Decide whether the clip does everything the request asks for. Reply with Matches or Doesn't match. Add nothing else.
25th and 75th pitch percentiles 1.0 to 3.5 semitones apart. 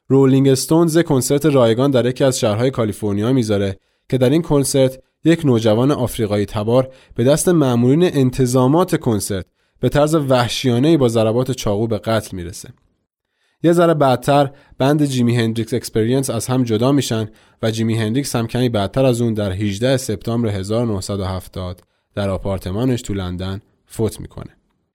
Doesn't match